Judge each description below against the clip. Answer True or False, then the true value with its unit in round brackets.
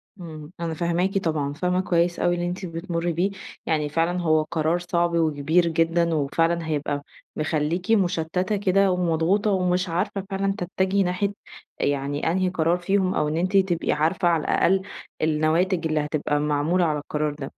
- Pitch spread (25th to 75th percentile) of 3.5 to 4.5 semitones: False (2.7 semitones)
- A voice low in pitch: False (170 Hz)